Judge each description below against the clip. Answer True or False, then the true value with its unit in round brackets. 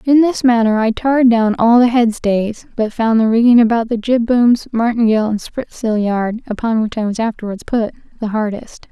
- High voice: True (230 Hz)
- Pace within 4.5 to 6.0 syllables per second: True (5.0 syllables/s)